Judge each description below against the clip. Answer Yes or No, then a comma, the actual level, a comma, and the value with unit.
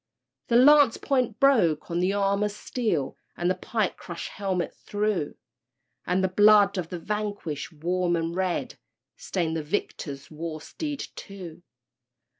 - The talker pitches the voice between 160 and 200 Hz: Yes, high, 190 Hz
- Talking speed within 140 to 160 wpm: Yes, average, 145 wpm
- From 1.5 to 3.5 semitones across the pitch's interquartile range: No, average, 3.9 semitones